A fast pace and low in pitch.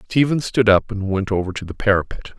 Yes: fast, 225 wpm; low, 105 Hz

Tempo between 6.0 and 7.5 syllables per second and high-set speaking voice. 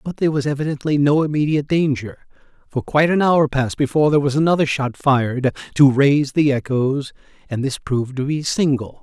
No: 6.1 syllables/s; medium, 140 Hz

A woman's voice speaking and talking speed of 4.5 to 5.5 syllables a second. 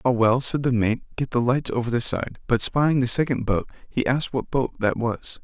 No: male; 5.2 syllables/s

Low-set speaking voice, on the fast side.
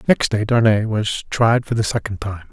Yes: low, 110 Hz; fast, 215 wpm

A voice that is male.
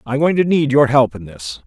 Yes: male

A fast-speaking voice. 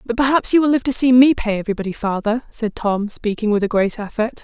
Yes: fast, 245 wpm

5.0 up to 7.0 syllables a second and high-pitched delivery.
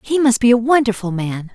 Yes: 5.5 syllables/s; high, 230 Hz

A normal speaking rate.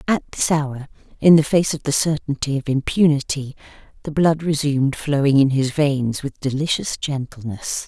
Yes: average, 160 wpm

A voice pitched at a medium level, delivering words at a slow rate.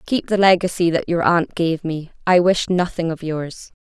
No: medium, 175 Hz; fast, 205 wpm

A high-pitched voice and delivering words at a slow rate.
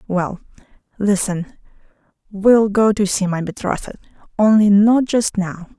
Yes: high, 200 Hz; slow, 125 wpm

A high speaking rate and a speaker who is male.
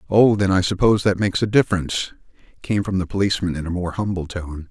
Yes: fast, 215 wpm; male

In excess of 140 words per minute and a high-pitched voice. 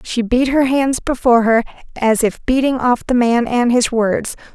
Yes: average, 200 wpm; high, 245 Hz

